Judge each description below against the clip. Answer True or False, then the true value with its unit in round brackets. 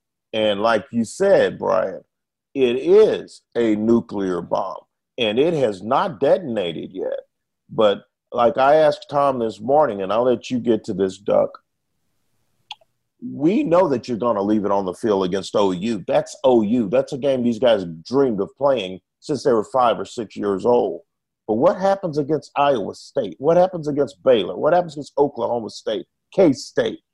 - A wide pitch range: True (6.3 semitones)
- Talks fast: False (175 wpm)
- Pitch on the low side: True (125 Hz)